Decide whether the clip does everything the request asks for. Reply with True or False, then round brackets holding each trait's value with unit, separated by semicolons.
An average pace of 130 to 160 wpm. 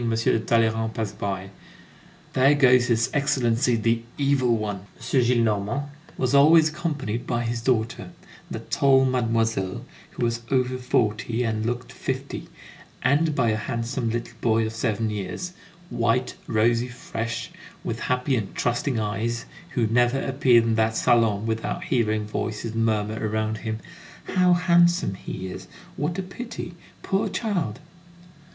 True (140 wpm)